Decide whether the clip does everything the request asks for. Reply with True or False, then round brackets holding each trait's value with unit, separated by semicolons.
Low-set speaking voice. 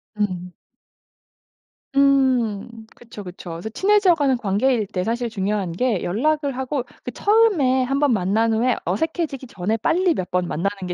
False (235 Hz)